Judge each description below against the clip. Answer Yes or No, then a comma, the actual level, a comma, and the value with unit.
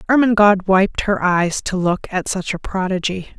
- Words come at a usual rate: Yes, average, 175 wpm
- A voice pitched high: Yes, high, 195 Hz